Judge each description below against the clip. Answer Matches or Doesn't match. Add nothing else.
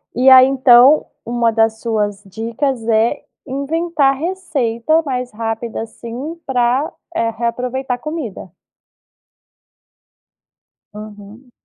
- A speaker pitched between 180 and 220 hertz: Doesn't match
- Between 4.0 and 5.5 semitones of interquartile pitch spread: Doesn't match